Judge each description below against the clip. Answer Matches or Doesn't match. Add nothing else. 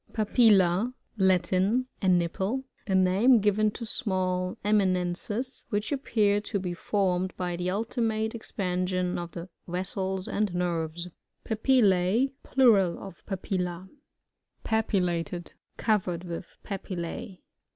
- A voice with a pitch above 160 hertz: Matches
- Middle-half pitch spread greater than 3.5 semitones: Doesn't match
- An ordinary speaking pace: Doesn't match